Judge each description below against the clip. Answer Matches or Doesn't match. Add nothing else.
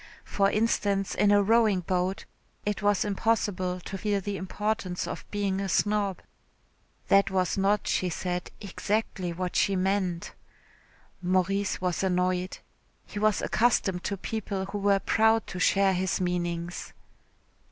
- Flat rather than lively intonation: Matches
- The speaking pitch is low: Doesn't match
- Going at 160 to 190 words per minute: Doesn't match